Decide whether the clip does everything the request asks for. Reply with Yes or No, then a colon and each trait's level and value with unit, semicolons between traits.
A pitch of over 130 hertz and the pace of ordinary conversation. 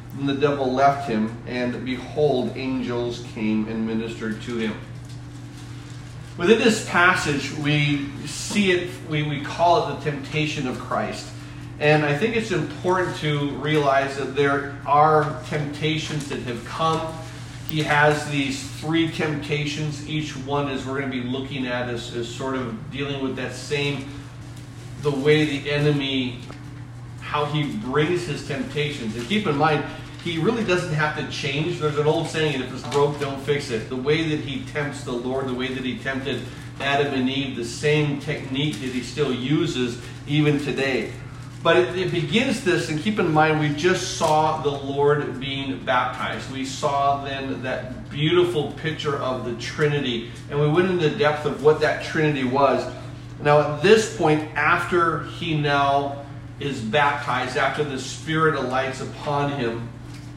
Yes: medium, 140 Hz; average, 165 wpm